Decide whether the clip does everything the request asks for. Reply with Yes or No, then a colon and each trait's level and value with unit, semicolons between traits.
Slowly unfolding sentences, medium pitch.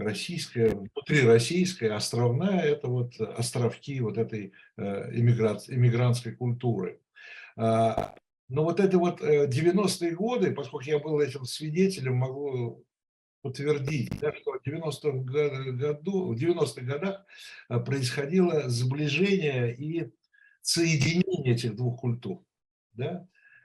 Yes: slow, 105 wpm; medium, 145 Hz